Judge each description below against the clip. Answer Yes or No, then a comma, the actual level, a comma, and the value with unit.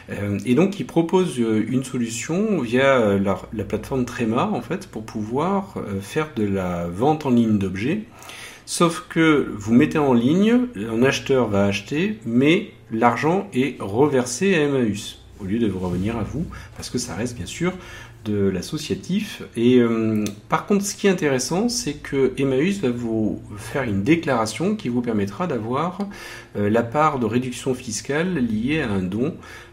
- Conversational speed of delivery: Yes, average, 170 wpm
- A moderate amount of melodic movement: No, wide, 6.2 semitones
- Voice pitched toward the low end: Yes, low, 125 Hz